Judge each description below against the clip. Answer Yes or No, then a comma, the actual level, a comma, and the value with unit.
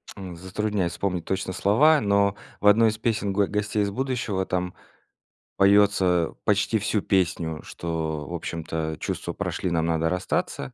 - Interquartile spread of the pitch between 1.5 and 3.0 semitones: No, average, 3.4 semitones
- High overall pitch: No, very low, 95 Hz